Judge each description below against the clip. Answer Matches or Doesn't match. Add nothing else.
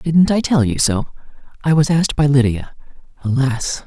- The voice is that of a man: Matches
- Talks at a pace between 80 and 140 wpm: Doesn't match